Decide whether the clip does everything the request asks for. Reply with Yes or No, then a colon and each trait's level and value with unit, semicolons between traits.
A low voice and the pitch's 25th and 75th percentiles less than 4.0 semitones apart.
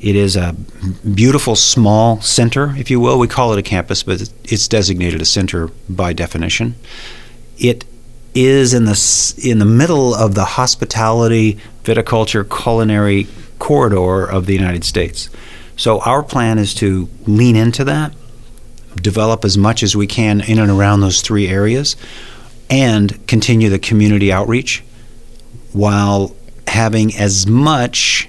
Yes: low, 110 Hz; average, 3.0 semitones